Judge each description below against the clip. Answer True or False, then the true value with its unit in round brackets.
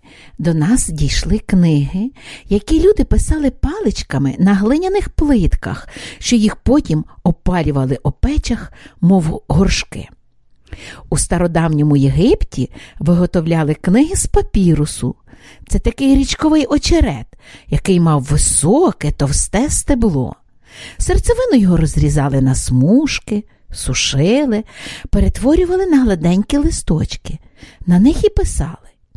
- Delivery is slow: True (100 wpm)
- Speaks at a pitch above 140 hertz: True (190 Hz)